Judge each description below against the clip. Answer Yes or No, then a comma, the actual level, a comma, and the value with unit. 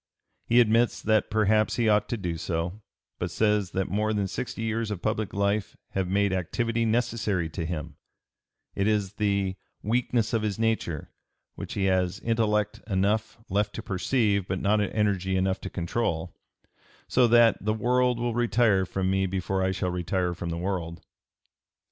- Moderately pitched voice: No, low, 100 Hz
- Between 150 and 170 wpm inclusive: Yes, average, 165 wpm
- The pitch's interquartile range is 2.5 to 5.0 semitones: Yes, average, 3.0 semitones